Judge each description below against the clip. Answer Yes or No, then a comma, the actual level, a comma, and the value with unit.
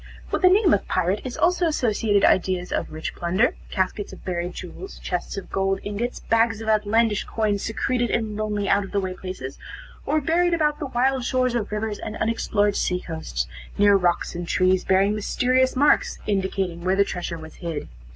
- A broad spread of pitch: No, average, 4.5 semitones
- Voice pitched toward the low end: No, high, 205 Hz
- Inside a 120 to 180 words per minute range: No, average, 190 wpm